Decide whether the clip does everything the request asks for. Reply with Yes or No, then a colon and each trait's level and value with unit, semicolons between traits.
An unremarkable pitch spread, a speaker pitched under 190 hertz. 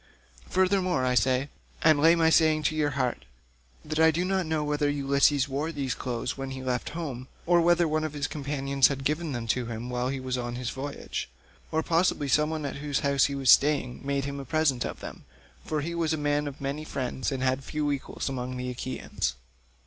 Yes: average, 3.1 semitones; medium, 140 Hz